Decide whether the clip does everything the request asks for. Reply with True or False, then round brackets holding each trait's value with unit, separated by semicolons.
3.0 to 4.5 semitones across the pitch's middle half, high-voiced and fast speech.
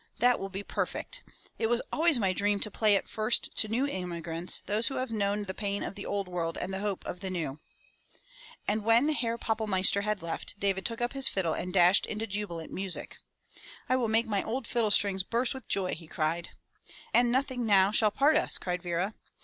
True (3.7 semitones; 205 Hz; 210 wpm)